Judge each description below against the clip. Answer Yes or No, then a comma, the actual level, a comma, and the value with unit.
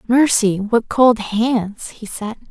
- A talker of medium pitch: No, high, 225 Hz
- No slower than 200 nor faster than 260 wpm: No, average, 145 wpm